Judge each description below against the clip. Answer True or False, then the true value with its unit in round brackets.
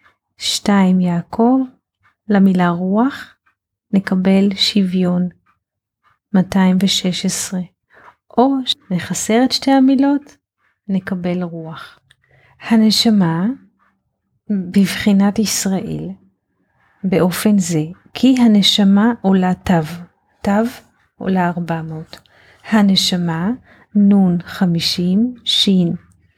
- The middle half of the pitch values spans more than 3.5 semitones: False (3.2 semitones)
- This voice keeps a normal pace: False (70 wpm)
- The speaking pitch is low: False (190 Hz)